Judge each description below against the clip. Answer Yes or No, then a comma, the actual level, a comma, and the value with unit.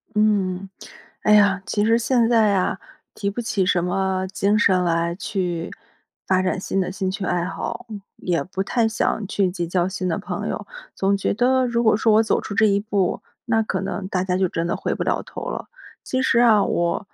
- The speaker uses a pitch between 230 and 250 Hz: No, high, 195 Hz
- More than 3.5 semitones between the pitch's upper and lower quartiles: No, average, 2.9 semitones